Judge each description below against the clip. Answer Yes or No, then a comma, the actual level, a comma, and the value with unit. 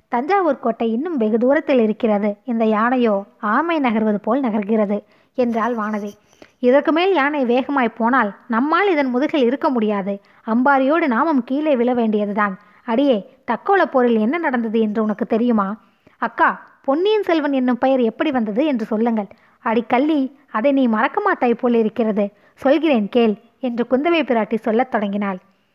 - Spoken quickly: Yes, fast, 140 wpm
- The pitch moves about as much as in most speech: Yes, average, 3.9 semitones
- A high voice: Yes, high, 240 Hz